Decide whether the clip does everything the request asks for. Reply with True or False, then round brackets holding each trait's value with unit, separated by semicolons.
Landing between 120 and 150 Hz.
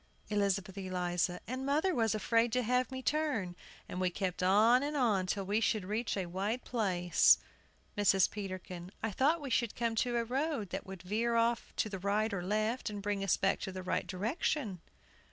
False (210 Hz)